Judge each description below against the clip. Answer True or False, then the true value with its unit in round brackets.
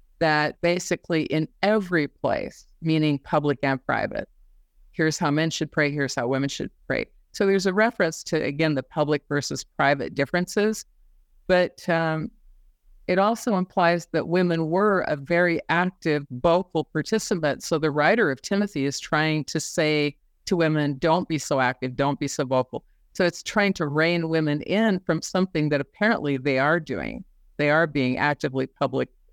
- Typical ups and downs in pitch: True (3.5 semitones)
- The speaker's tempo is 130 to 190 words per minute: True (165 wpm)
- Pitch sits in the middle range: True (160 Hz)